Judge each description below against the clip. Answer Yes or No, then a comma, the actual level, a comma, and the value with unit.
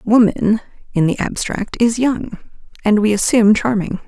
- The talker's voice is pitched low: No, high, 215 Hz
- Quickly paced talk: No, average, 145 wpm